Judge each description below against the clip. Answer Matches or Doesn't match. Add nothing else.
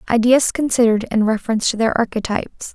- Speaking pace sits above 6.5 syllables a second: Matches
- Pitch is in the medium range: Doesn't match